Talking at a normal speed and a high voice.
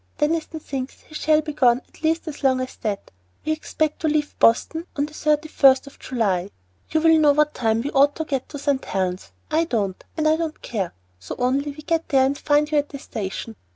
No: fast, 220 wpm; very high, 290 Hz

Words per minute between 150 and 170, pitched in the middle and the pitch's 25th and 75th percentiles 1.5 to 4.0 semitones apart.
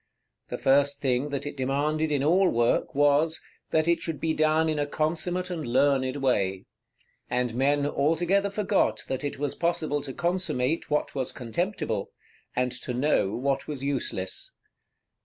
Yes: average, 155 wpm; medium, 145 Hz; average, 3.5 semitones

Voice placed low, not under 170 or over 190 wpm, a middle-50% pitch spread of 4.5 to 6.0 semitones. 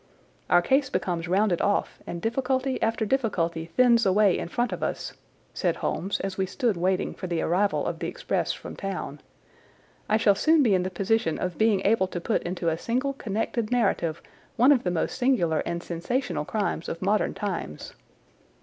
No: high, 200 Hz; average, 185 wpm; average, 5.1 semitones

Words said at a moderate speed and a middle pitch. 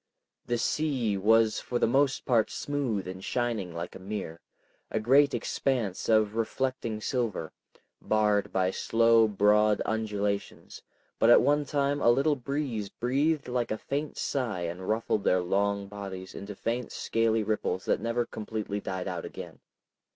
No: average, 150 wpm; low, 110 Hz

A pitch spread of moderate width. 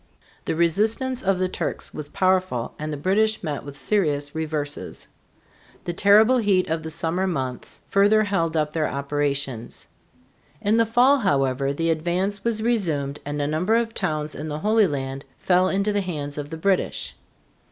No: wide, 5.7 semitones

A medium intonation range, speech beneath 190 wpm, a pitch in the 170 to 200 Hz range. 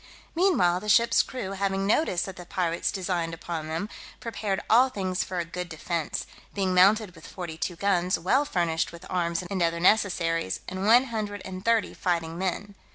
Yes: average, 3.1 semitones; average, 180 wpm; medium, 185 Hz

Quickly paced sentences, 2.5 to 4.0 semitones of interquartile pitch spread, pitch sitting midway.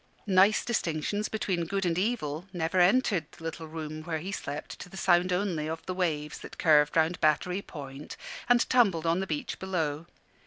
No: average, 185 wpm; average, 3.4 semitones; medium, 170 Hz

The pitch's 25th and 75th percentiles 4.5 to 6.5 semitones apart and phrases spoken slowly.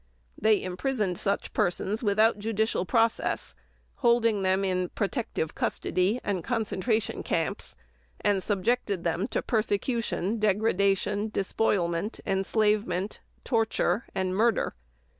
No: average, 2.9 semitones; slow, 105 wpm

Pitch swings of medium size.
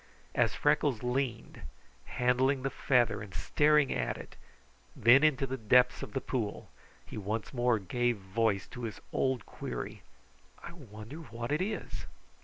Yes: average, 3.8 semitones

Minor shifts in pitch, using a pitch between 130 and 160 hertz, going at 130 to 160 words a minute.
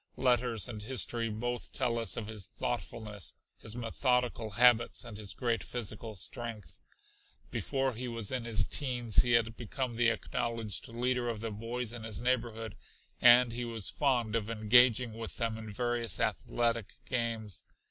No: narrow, 1.7 semitones; low, 115 Hz; average, 155 wpm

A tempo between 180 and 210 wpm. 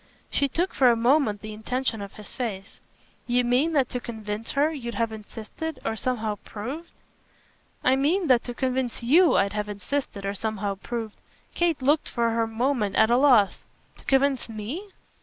Yes: average, 185 wpm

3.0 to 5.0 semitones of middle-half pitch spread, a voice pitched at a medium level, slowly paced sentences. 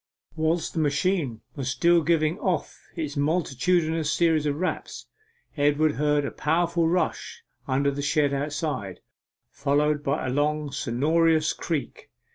No: narrow, 2.5 semitones; medium, 150 Hz; slow, 130 wpm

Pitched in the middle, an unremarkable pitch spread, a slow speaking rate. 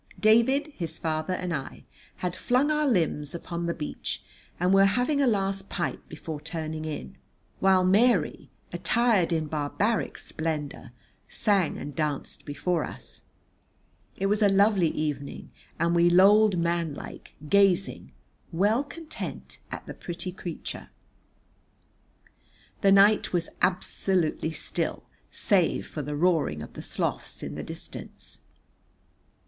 Yes: medium, 180 Hz; average, 4.2 semitones; slow, 130 wpm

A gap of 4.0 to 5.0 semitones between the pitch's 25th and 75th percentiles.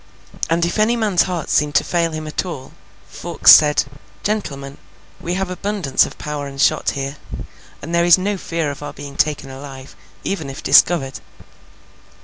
Yes: average, 4.4 semitones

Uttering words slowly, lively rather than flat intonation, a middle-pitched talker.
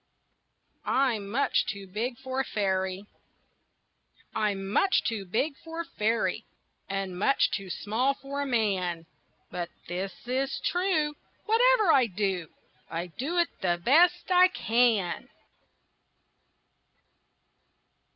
No: slow, 115 wpm; wide, 6.5 semitones; high, 230 Hz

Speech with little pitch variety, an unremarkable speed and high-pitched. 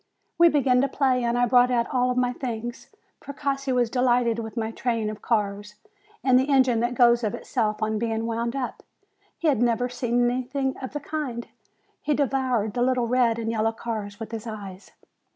Yes: narrow, 2.3 semitones; average, 190 wpm; high, 240 Hz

